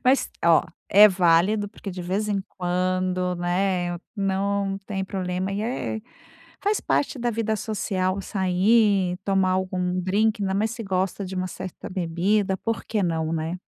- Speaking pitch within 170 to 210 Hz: Yes, high, 190 Hz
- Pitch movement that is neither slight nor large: No, narrow, 2.2 semitones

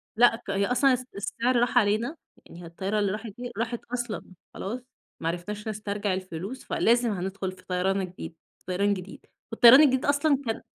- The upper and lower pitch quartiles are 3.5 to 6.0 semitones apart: Yes, average, 4.2 semitones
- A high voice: Yes, high, 210 Hz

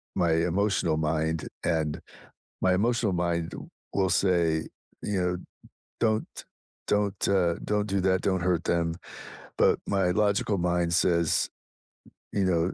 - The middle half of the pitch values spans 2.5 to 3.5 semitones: Yes, average, 2.8 semitones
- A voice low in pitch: Yes, very low, 90 Hz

